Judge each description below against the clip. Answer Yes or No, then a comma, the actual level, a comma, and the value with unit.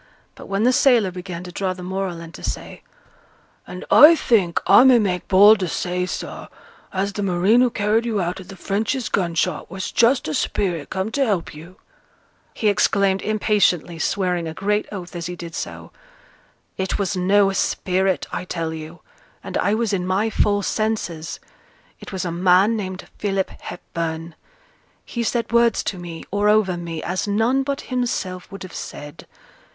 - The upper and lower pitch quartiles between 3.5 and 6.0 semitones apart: No, average, 3.0 semitones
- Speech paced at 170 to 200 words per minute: Yes, average, 180 wpm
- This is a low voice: No, high, 190 Hz